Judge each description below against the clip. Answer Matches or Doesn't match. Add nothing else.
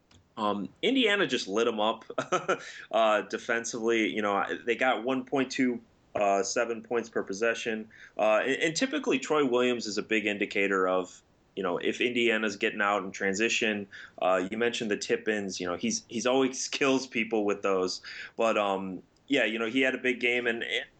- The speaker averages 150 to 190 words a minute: Matches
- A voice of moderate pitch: Doesn't match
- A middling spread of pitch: Matches